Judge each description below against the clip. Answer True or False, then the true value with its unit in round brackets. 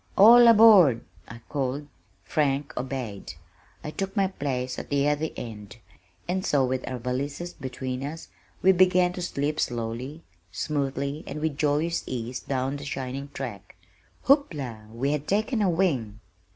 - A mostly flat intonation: False (4.7 semitones)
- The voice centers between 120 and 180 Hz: True (140 Hz)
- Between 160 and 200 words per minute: False (145 wpm)